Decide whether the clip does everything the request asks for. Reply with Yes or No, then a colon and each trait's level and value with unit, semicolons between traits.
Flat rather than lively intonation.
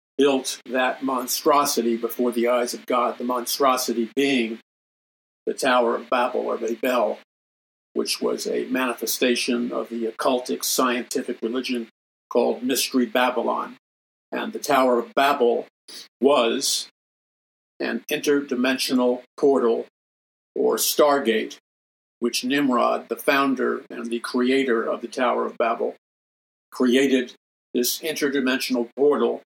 Yes: narrow, 2.1 semitones